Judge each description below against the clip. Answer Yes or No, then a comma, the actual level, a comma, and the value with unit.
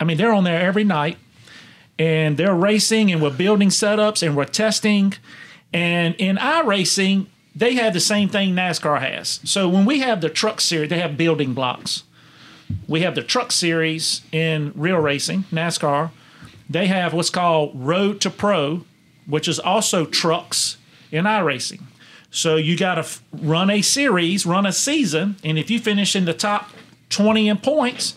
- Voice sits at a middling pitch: Yes, medium, 175 Hz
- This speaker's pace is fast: No, average, 170 wpm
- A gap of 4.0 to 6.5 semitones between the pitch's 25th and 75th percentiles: Yes, average, 4.4 semitones